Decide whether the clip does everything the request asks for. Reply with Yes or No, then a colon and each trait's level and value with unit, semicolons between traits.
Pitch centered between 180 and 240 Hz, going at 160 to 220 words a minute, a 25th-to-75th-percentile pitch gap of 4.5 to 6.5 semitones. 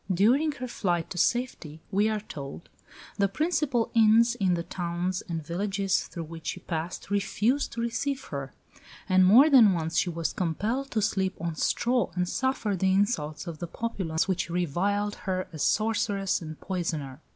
Yes: high, 190 Hz; average, 170 wpm; average, 5.0 semitones